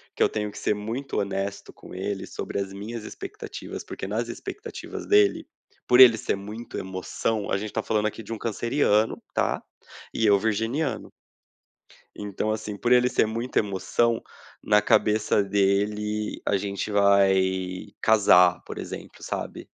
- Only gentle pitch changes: Yes, narrow, 2.2 semitones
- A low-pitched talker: Yes, low, 105 Hz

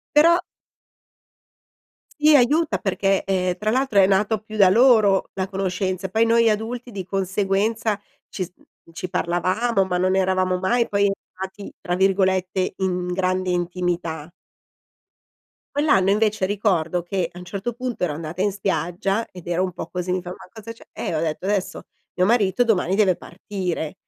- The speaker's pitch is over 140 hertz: Yes, high, 190 Hz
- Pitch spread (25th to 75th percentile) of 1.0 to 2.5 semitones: No, average, 2.9 semitones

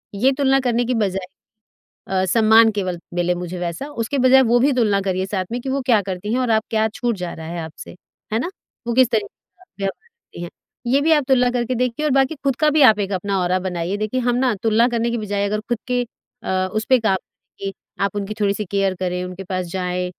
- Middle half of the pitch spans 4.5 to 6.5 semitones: Yes, average, 4.8 semitones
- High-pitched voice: Yes, high, 215 Hz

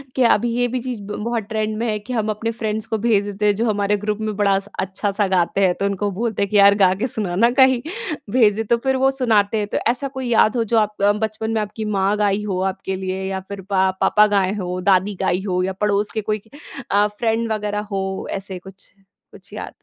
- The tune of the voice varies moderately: No, narrow, 2.1 semitones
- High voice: Yes, high, 210 Hz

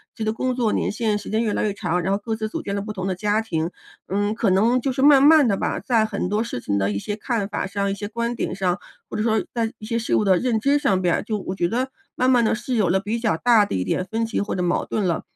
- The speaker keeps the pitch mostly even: No, average, 3.2 semitones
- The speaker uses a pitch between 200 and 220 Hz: Yes, high, 215 Hz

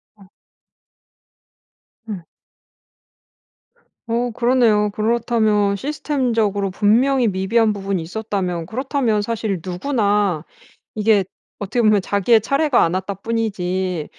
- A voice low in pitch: No, high, 210 Hz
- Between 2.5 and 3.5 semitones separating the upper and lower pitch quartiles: Yes, average, 3.2 semitones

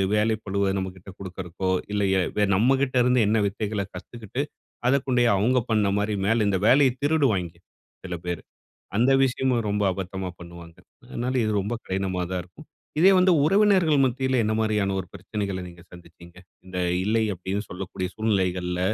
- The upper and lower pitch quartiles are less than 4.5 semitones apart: No, average, 5.1 semitones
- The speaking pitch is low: Yes, low, 105 Hz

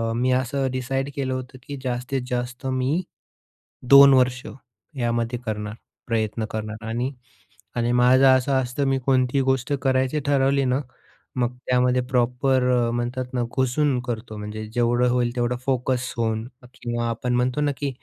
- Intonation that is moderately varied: No, narrow, 1.7 semitones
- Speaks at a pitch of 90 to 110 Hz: No, low, 125 Hz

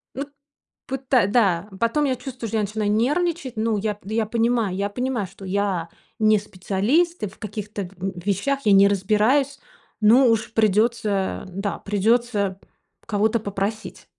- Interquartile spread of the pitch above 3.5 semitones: No, average, 3.2 semitones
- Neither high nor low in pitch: No, high, 215 Hz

